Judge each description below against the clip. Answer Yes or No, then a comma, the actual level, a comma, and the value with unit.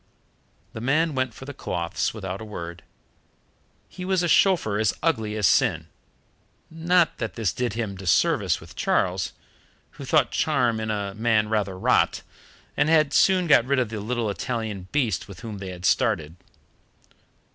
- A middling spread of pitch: No, wide, 5.9 semitones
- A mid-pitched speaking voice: No, low, 110 Hz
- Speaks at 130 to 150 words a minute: No, average, 165 wpm